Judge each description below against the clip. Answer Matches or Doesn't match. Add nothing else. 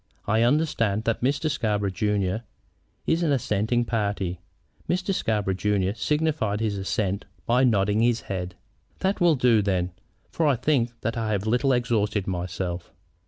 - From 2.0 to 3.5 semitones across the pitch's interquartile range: Doesn't match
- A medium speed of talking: Matches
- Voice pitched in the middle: Doesn't match